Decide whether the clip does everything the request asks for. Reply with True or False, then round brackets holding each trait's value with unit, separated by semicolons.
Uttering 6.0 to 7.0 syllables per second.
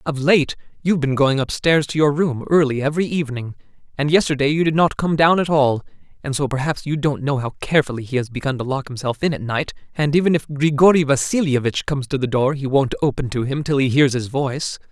True (6.1 syllables/s)